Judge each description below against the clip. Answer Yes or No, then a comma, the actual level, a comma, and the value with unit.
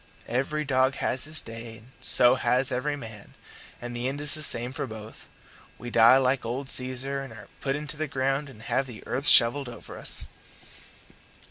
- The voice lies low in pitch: Yes, low, 130 Hz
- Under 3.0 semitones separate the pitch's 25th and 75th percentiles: Yes, narrow, 2.6 semitones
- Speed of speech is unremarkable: Yes, average, 190 wpm